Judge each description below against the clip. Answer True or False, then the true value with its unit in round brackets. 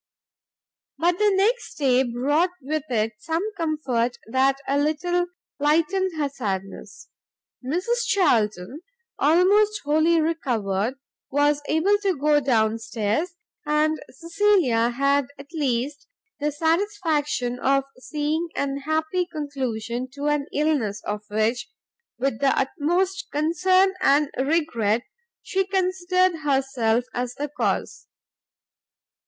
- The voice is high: True (295 Hz)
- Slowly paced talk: True (115 wpm)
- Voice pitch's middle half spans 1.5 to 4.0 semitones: False (5.0 semitones)